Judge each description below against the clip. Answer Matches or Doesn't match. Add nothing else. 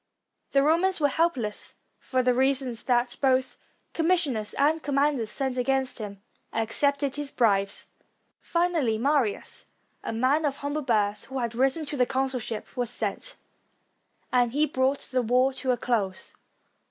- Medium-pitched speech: Doesn't match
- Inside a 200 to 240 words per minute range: Doesn't match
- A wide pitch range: Doesn't match